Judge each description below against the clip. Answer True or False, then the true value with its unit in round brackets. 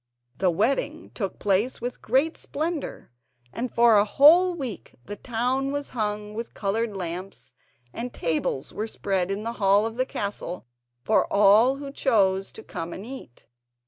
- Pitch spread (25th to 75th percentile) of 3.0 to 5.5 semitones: True (4.8 semitones)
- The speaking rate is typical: True (160 wpm)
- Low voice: False (220 Hz)